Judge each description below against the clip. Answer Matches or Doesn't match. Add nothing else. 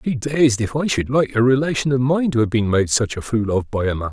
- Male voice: Matches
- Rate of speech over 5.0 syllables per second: Matches